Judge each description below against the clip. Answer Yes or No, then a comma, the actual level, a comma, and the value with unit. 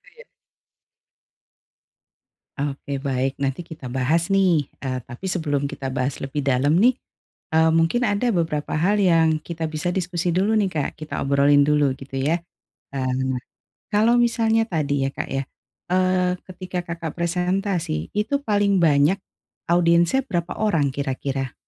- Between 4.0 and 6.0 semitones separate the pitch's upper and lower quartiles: Yes, average, 4.8 semitones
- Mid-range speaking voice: Yes, medium, 165 Hz